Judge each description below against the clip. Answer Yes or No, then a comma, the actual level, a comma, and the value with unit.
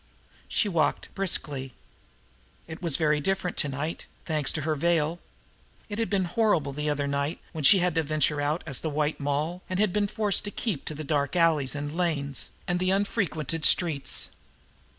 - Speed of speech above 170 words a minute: Yes, average, 180 wpm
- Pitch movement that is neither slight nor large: Yes, average, 3.8 semitones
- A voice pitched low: No, medium, 160 Hz